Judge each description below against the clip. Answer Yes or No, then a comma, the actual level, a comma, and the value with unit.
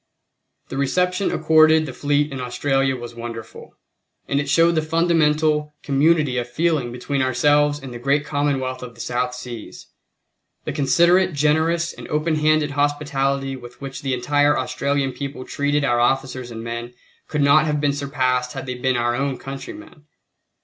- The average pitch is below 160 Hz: Yes, medium, 140 Hz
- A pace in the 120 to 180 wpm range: Yes, average, 165 wpm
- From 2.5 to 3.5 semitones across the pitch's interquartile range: Yes, average, 3.0 semitones